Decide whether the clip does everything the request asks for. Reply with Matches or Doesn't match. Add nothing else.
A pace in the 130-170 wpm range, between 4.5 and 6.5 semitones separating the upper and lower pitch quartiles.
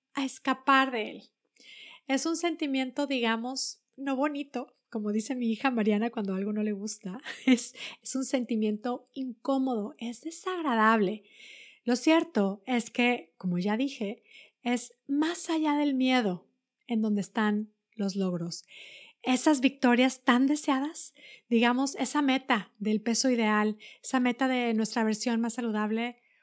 Doesn't match